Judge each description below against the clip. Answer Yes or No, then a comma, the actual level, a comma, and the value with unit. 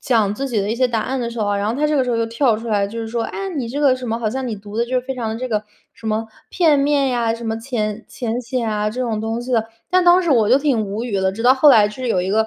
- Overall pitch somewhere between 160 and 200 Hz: No, high, 230 Hz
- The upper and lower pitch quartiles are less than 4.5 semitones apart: Yes, average, 3.0 semitones